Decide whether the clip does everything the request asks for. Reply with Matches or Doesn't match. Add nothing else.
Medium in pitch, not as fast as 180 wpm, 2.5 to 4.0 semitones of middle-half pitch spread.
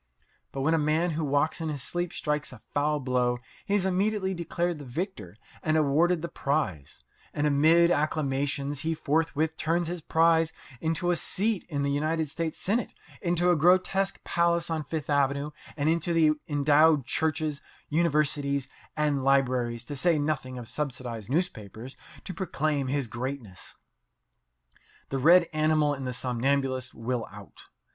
Matches